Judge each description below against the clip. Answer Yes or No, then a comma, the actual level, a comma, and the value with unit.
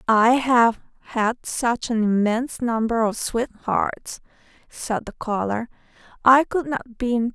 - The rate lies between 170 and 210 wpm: No, average, 145 wpm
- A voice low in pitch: No, high, 235 Hz